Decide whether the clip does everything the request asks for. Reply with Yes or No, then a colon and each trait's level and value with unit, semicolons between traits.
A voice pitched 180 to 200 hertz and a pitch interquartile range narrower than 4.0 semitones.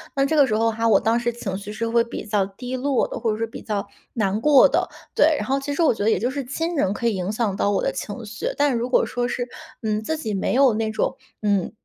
No: high, 230 Hz; average, 3.6 semitones